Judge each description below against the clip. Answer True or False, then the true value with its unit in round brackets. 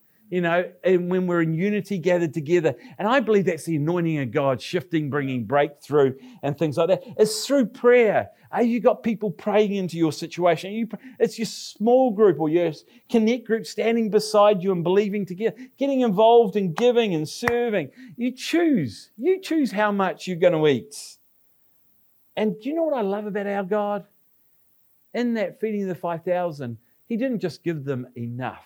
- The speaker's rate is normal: True (180 wpm)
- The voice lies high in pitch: True (200 Hz)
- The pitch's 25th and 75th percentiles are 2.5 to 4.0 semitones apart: False (5.1 semitones)